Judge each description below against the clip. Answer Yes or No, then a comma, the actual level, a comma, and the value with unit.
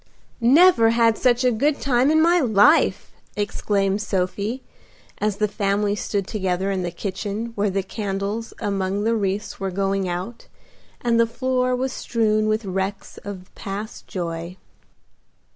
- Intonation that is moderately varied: Yes, average, 3.0 semitones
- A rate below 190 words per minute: Yes, average, 145 wpm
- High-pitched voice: Yes, high, 210 Hz